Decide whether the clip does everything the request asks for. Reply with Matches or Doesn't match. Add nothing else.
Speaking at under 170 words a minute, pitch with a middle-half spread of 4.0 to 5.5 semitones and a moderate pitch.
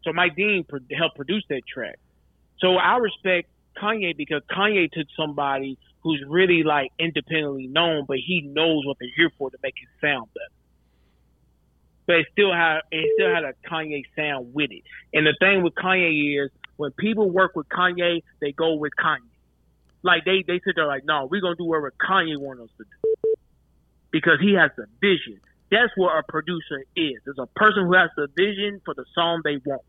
Doesn't match